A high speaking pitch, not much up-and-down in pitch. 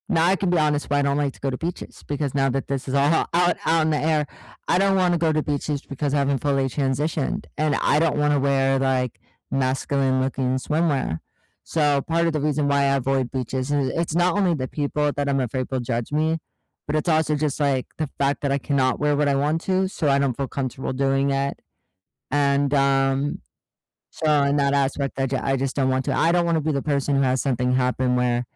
No: medium, 140 Hz; narrow, 2.2 semitones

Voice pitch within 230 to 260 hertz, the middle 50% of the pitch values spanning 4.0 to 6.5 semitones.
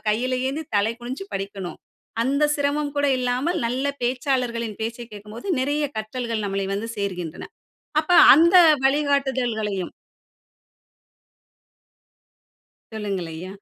Yes: high, 240 Hz; average, 5.3 semitones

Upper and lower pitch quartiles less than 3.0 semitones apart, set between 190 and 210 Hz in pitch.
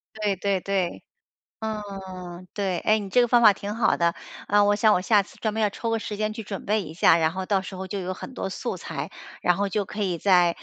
Yes: narrow, 2.4 semitones; high, 200 Hz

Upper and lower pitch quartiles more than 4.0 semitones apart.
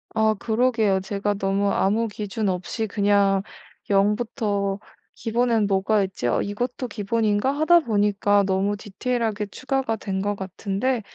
No: narrow, 2.4 semitones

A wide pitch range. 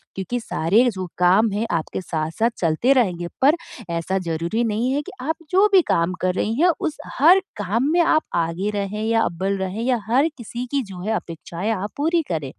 Yes: wide, 6.1 semitones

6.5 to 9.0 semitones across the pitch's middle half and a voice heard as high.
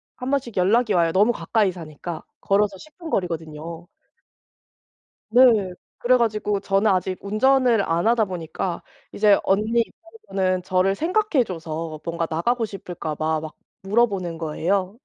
No: wide, 5.4 semitones; high, 195 Hz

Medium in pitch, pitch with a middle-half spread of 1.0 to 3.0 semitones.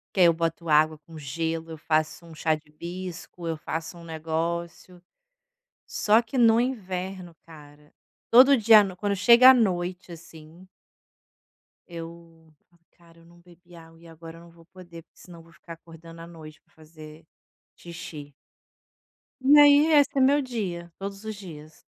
Yes: medium, 170 Hz; narrow, 2.6 semitones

